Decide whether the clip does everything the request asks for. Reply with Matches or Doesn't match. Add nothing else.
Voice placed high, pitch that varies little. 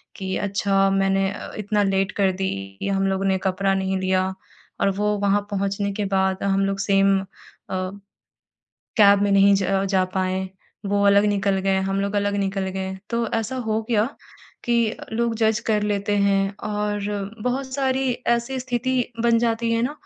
Matches